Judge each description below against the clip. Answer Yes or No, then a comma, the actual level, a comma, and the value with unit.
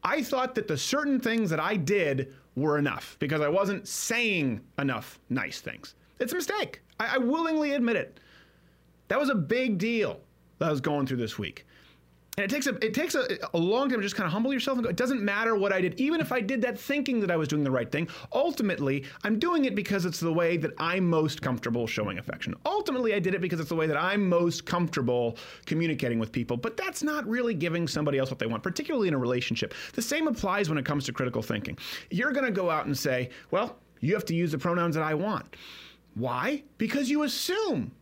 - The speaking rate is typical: No, fast, 235 wpm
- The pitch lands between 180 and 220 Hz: Yes, medium, 185 Hz